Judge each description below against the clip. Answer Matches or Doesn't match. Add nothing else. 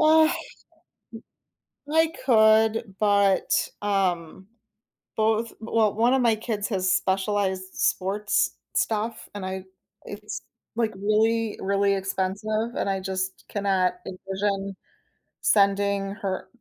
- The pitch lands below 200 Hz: Doesn't match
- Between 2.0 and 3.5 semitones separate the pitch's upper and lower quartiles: Matches